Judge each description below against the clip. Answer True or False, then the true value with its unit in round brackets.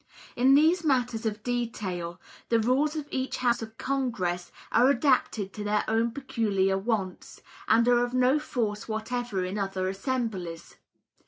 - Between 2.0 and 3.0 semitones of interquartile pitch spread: False (4.4 semitones)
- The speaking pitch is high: True (230 Hz)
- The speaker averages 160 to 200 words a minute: False (150 wpm)